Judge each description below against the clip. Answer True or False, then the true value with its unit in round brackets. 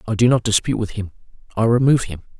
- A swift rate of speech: True (225 wpm)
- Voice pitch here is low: True (110 Hz)